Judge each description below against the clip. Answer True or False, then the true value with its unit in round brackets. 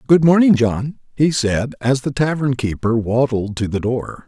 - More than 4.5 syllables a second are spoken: False (4.4 syllables/s)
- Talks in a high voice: False (130 Hz)